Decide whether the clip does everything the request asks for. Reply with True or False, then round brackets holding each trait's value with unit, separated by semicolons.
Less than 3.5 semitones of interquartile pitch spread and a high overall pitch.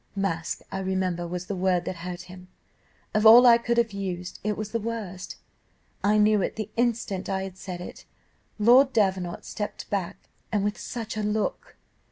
True (3.1 semitones; 200 Hz)